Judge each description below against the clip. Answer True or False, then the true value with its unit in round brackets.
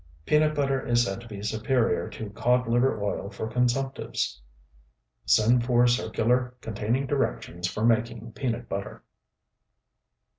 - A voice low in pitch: True (120 Hz)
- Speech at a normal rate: False (120 wpm)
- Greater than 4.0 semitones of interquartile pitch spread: False (2.4 semitones)